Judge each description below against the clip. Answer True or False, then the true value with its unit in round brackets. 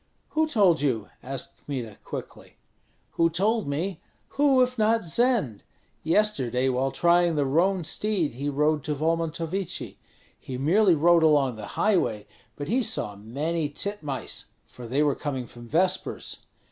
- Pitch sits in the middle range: True (160 Hz)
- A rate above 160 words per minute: False (145 wpm)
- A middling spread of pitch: False (6.3 semitones)